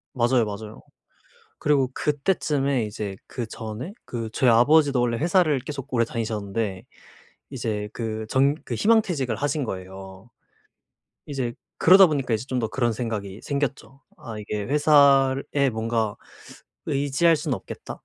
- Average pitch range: Yes, average, 4.4 semitones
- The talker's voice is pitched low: Yes, low, 125 Hz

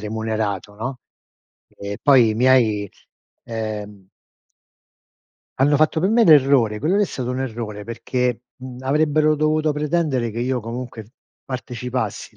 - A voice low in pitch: Yes, low, 125 Hz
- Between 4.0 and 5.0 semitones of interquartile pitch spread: Yes, average, 4.6 semitones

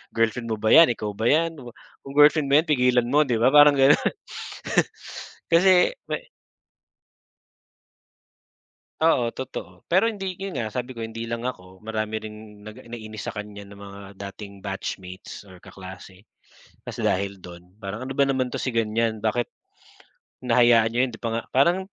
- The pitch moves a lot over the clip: No, average, 4.6 semitones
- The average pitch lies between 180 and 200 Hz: No, low, 115 Hz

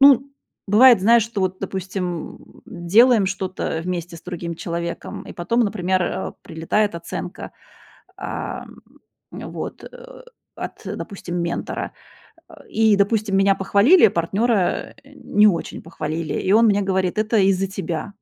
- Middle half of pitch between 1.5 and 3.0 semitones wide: No, average, 3.7 semitones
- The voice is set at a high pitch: Yes, high, 195 Hz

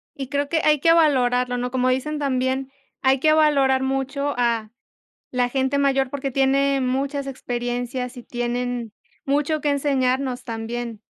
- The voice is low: No, very high, 265 Hz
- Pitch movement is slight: Yes, narrow, 2.2 semitones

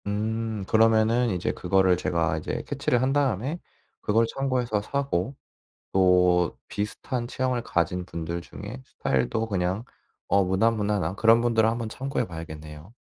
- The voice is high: No, low, 105 Hz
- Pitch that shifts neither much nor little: Yes, average, 4.5 semitones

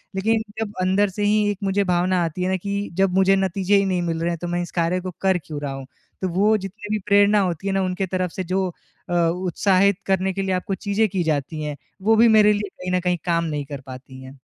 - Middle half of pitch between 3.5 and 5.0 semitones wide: No, narrow, 2.5 semitones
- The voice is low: No, medium, 185 Hz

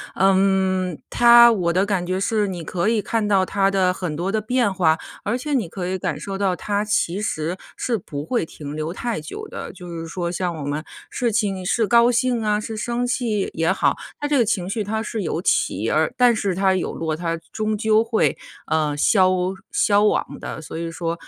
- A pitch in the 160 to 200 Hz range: Yes, high, 195 Hz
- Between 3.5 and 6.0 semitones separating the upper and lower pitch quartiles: Yes, average, 4.2 semitones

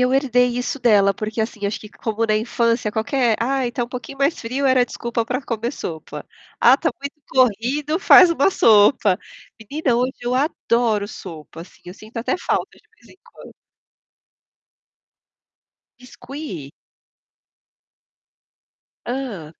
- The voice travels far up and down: No, average, 3.6 semitones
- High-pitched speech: Yes, high, 240 Hz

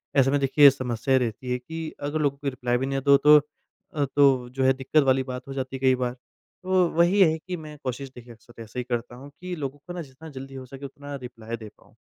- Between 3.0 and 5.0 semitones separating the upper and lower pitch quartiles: No, narrow, 2.6 semitones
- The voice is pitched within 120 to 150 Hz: Yes, low, 135 Hz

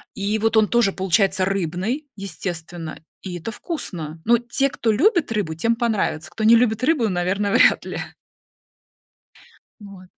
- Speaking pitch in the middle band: No, high, 205 Hz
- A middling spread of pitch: Yes, average, 4.2 semitones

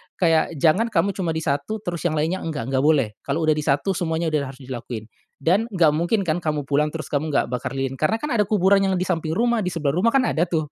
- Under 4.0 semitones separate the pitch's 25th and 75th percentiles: No, average, 4.3 semitones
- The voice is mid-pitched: Yes, medium, 160 Hz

